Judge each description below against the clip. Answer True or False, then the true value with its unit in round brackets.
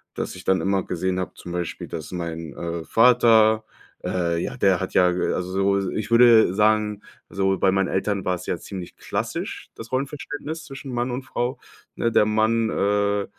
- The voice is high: False (100 Hz)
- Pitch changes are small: False (3.9 semitones)